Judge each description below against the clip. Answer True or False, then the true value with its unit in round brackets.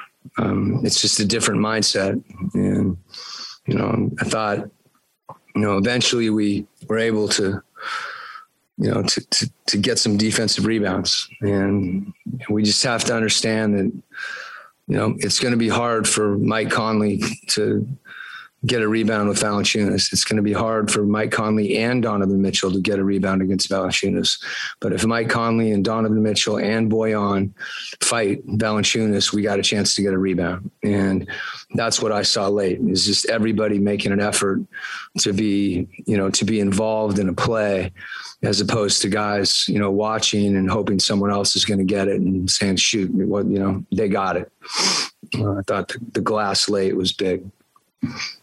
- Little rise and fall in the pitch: True (1.8 semitones)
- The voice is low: True (105 Hz)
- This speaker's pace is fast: False (175 wpm)